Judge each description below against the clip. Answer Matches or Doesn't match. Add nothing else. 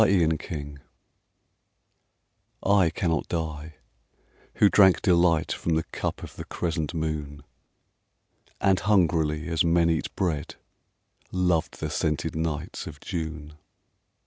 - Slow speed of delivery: Matches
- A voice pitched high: Doesn't match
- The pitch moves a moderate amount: Doesn't match